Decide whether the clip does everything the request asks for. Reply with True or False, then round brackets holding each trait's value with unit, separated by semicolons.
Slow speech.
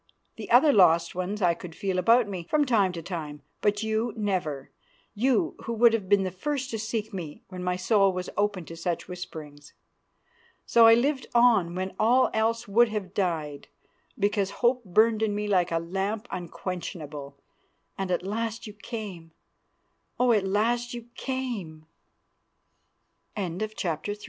False (155 wpm)